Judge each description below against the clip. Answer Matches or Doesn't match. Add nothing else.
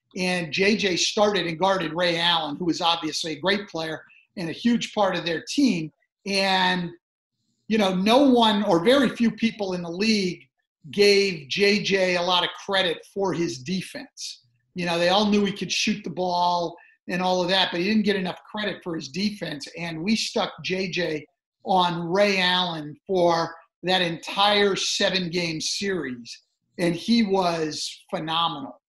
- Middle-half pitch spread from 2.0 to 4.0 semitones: Matches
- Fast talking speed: Doesn't match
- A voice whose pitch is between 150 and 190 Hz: Matches